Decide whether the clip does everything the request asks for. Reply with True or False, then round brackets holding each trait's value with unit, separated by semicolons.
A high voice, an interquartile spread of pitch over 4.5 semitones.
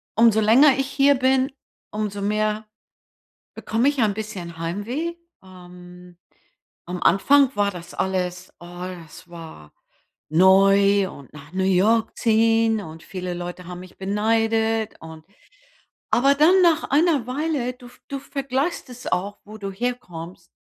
True (205 Hz; 5.5 semitones)